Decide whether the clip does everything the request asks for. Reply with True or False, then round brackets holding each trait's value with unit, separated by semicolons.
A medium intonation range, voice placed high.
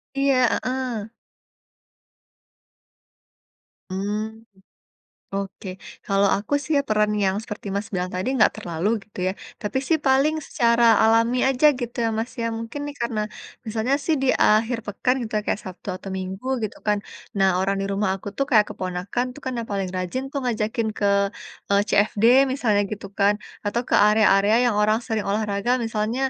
True (3.3 semitones; 215 Hz)